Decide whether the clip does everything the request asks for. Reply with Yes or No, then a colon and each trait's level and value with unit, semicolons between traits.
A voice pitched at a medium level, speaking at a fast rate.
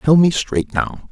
Yes: medium, 145 Hz; fast, 215 wpm